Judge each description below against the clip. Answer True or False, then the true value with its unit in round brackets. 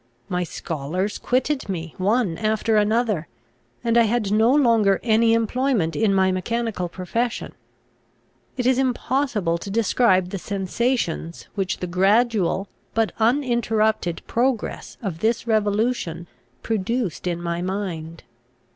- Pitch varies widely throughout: False (4.3 semitones)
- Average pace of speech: False (120 wpm)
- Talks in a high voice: True (215 Hz)